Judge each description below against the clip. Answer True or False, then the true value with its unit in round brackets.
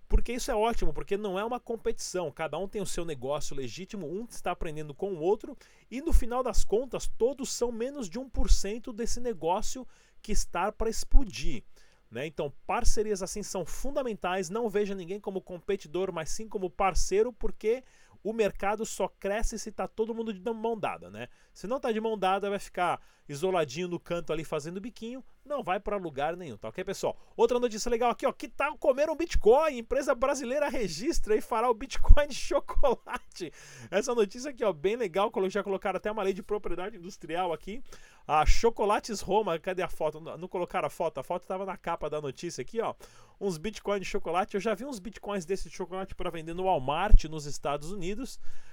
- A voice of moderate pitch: False (205 Hz)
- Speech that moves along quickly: True (200 wpm)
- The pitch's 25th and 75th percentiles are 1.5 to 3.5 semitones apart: False (4.6 semitones)